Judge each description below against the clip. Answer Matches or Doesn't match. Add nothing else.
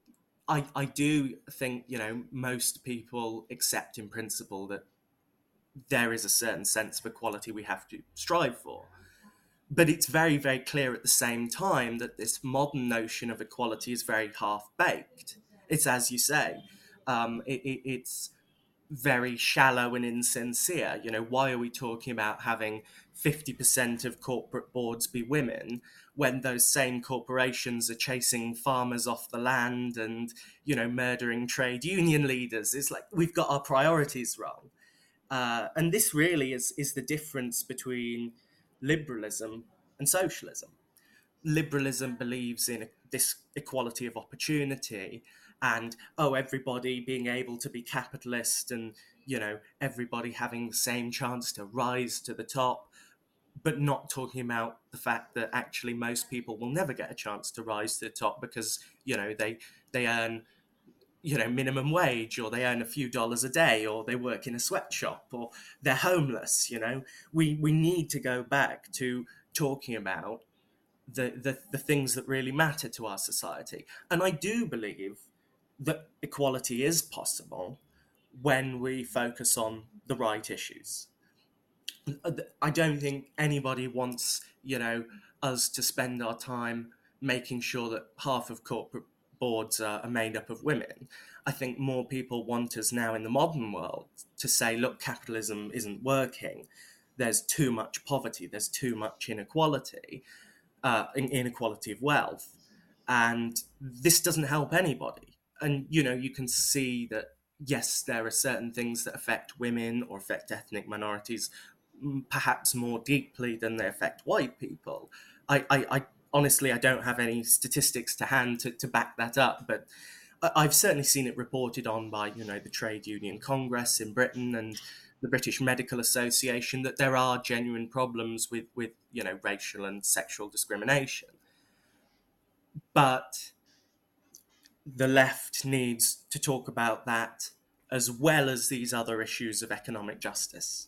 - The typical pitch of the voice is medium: Doesn't match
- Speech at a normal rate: Matches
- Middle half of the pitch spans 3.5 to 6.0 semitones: Doesn't match